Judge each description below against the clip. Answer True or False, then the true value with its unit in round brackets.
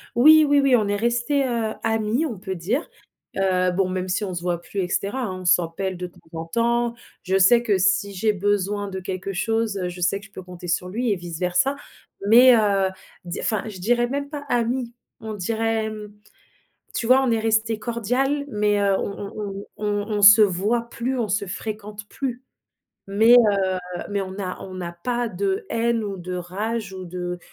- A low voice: False (210 Hz)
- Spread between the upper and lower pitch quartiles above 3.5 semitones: True (3.9 semitones)